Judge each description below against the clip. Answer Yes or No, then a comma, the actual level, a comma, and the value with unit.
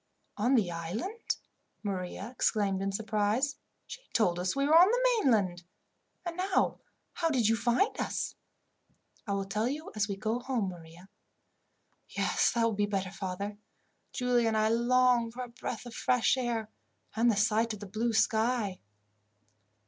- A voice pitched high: Yes, high, 225 Hz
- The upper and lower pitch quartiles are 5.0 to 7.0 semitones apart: No, average, 3.7 semitones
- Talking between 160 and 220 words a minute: Yes, average, 165 wpm